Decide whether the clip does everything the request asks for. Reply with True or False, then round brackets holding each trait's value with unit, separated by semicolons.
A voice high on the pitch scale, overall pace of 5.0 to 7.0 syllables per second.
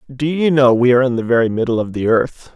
False (125 Hz; 6.3 syllables/s)